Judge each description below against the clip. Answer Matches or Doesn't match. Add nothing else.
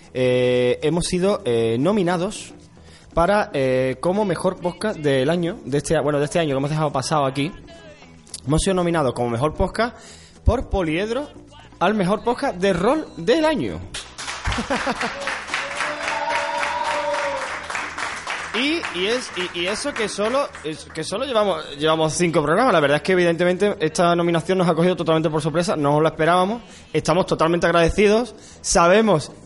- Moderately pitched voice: Matches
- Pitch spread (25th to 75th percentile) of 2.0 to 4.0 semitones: Doesn't match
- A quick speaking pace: Doesn't match